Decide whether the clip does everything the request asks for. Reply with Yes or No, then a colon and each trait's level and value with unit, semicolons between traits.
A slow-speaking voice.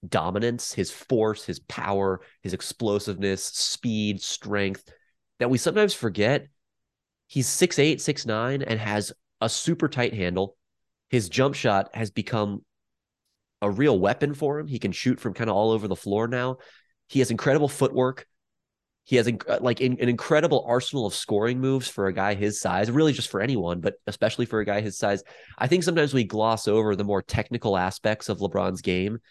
No: average, 180 wpm